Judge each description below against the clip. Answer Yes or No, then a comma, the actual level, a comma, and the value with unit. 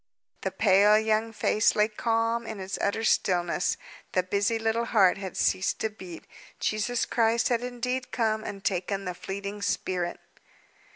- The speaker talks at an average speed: Yes, average, 155 wpm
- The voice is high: Yes, high, 210 Hz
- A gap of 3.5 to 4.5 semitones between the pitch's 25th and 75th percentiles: No, average, 2.9 semitones